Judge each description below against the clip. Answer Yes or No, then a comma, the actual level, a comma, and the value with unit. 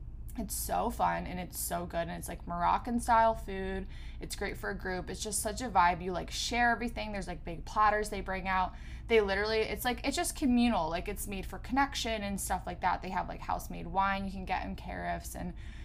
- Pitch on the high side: Yes, high, 195 Hz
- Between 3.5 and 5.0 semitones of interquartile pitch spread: Yes, average, 4.3 semitones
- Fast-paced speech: Yes, fast, 235 wpm